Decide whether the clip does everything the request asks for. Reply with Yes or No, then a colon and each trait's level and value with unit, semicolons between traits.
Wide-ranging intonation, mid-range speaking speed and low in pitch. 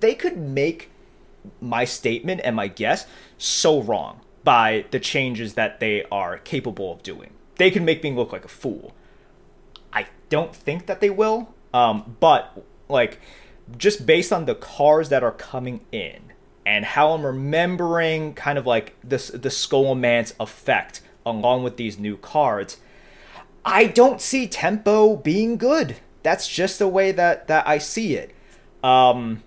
No: wide, 8.3 semitones; average, 155 wpm; medium, 150 Hz